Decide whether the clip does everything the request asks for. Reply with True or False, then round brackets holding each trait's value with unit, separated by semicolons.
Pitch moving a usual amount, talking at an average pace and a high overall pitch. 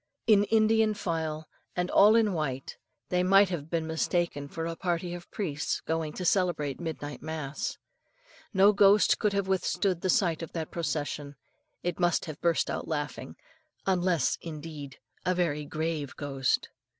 False (3.6 semitones; 155 wpm; 170 Hz)